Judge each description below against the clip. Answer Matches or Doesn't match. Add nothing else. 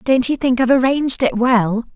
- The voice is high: Matches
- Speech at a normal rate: Doesn't match